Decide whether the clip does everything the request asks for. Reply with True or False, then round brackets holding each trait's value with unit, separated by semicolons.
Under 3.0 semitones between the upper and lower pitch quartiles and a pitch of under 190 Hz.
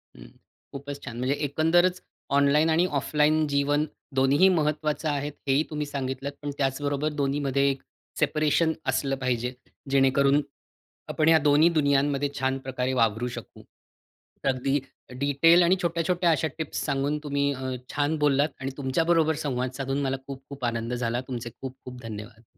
True (2.4 semitones; 140 Hz)